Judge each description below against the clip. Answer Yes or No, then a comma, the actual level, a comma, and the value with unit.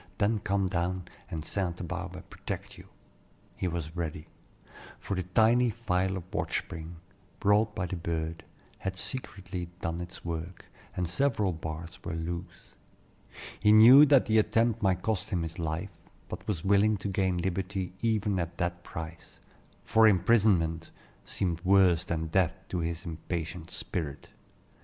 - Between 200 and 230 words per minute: No, average, 150 wpm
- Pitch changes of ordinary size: Yes, average, 3.4 semitones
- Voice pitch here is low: Yes, very low, 90 Hz